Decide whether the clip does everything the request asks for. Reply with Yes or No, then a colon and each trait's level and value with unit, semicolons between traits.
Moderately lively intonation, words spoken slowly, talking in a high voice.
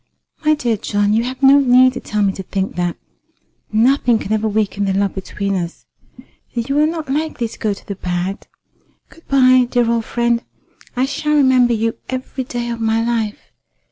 No: average, 4.0 semitones; average, 195 wpm; high, 235 Hz